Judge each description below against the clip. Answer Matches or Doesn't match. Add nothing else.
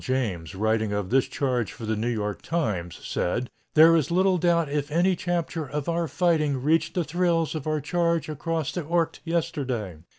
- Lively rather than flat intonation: Matches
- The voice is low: Doesn't match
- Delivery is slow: Doesn't match